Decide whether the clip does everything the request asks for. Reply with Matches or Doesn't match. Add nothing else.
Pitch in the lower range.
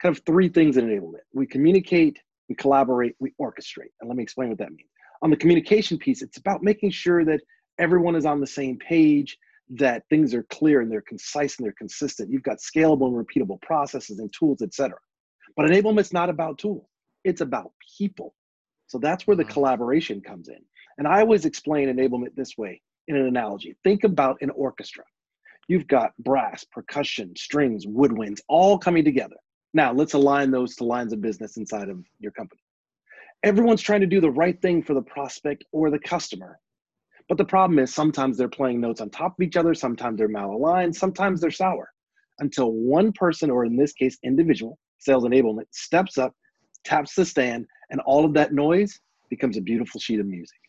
Doesn't match